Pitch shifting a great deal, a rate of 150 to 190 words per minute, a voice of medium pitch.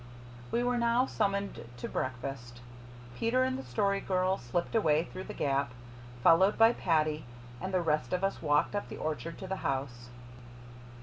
Yes: wide, 6.3 semitones; average, 170 wpm; medium, 180 Hz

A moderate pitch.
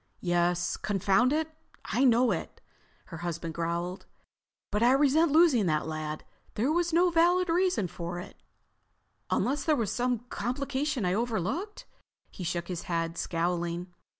No: high, 210 Hz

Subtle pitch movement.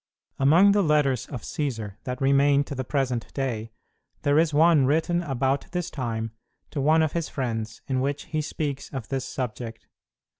No: average, 3.3 semitones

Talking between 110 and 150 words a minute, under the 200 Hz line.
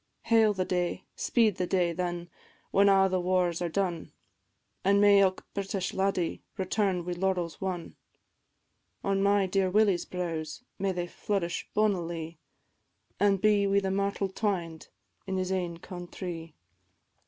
Yes: average, 140 wpm; medium, 185 Hz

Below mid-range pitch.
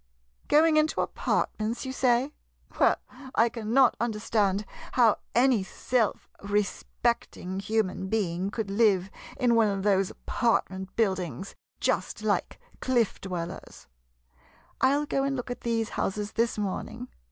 No: high, 220 Hz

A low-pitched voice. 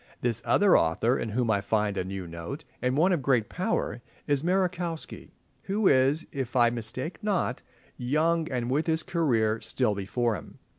Yes: low, 130 Hz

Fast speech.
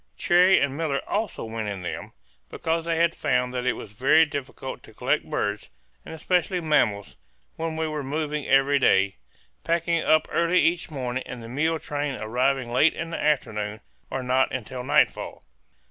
No: average, 175 wpm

